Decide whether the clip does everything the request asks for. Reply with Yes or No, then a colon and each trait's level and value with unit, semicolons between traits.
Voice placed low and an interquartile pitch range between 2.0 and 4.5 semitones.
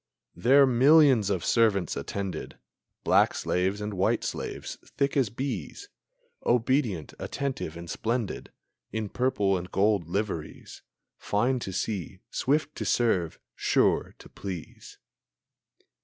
No: low, 105 Hz; wide, 5.4 semitones